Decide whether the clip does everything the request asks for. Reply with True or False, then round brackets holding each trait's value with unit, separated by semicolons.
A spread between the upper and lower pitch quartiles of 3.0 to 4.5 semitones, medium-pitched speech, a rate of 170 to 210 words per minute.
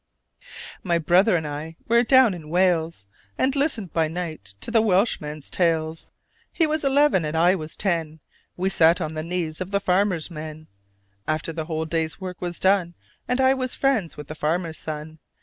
True (4.0 semitones; 170 Hz; 185 wpm)